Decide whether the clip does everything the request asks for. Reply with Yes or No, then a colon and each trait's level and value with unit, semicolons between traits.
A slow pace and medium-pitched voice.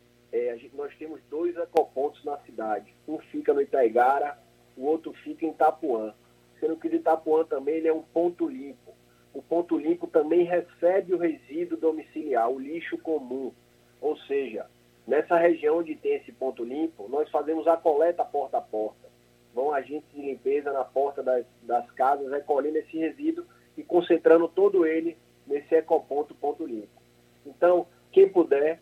No: average, 160 wpm; medium, 160 Hz